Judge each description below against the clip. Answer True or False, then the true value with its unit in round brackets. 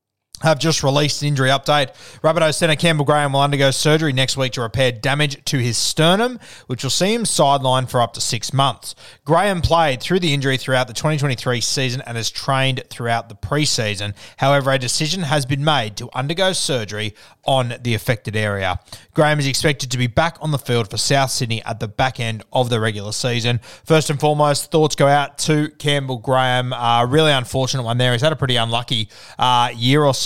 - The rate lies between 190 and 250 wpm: True (200 wpm)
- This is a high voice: False (130 Hz)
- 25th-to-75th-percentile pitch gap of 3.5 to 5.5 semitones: True (3.8 semitones)